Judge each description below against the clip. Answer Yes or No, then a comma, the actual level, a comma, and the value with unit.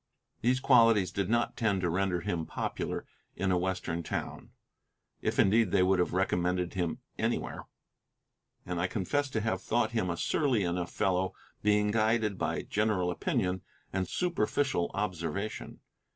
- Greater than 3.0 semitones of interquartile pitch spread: Yes, average, 3.6 semitones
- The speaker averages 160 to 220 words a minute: No, average, 150 wpm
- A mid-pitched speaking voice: No, very low, 95 Hz